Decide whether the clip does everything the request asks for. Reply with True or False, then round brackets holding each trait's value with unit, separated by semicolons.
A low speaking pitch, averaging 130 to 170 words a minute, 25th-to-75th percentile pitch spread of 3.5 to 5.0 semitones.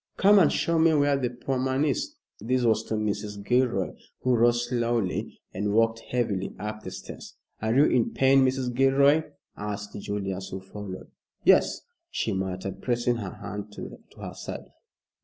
True (115 Hz; 165 wpm; 4.2 semitones)